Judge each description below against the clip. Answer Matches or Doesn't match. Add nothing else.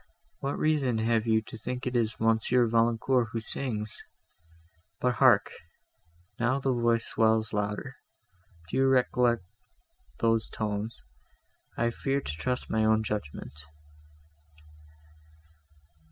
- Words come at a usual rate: Doesn't match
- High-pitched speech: Doesn't match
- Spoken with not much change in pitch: Matches